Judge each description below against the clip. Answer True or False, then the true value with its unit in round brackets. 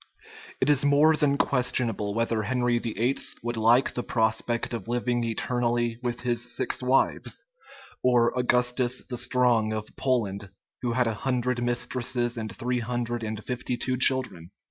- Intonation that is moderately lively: False (1.6 semitones)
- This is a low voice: True (120 Hz)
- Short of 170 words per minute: True (150 wpm)